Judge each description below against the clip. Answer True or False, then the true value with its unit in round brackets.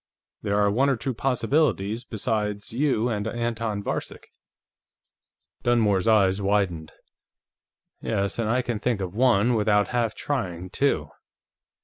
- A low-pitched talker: True (110 Hz)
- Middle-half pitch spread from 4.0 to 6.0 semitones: False (3.1 semitones)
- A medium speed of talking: False (125 wpm)